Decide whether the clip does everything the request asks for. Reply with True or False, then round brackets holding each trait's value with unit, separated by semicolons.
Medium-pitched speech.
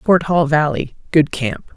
True (160 Hz)